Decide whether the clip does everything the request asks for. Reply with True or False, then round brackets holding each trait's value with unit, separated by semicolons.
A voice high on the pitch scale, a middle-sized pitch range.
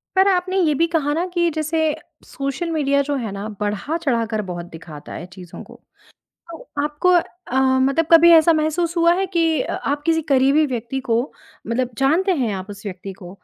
False (290 Hz; 6.6 semitones)